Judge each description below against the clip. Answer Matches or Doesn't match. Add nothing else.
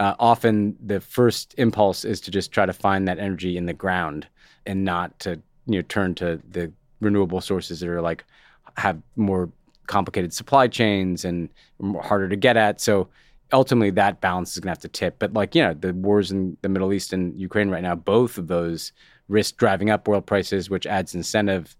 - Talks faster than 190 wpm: Matches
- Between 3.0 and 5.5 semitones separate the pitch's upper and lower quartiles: Doesn't match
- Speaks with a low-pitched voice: Matches